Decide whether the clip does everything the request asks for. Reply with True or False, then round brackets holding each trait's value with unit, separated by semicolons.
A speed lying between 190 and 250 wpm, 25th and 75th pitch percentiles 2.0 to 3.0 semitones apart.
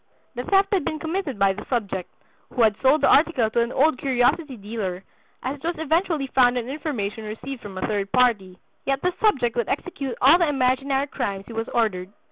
False (205 wpm; 5.2 semitones)